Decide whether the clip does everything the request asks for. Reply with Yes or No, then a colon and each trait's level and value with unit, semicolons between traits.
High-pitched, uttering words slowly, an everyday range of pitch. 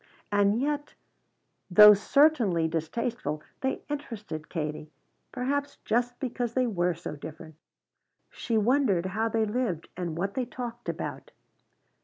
No: high, 215 Hz; slow, 125 wpm; wide, 6.3 semitones